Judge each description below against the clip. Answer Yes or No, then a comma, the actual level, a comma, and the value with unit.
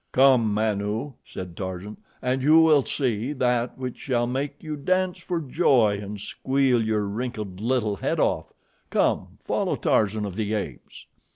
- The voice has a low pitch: Yes, low, 120 Hz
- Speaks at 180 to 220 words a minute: No, average, 155 wpm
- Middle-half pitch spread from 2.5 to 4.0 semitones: No, average, 4.6 semitones